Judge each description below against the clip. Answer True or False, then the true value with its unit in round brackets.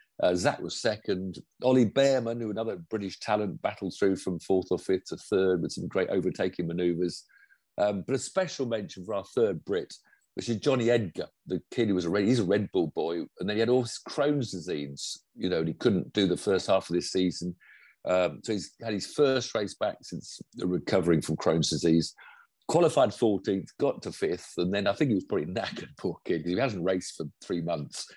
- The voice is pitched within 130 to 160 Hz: False (95 Hz)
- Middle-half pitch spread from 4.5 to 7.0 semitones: True (4.8 semitones)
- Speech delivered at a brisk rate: True (215 wpm)